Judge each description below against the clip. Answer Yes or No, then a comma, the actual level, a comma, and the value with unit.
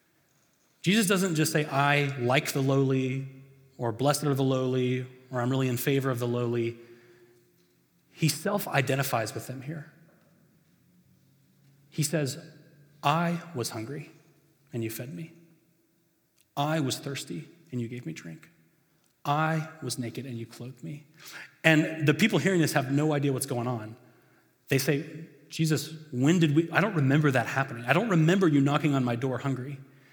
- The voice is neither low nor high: Yes, medium, 145 Hz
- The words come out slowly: No, average, 165 wpm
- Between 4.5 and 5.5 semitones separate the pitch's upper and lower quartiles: No, average, 3.7 semitones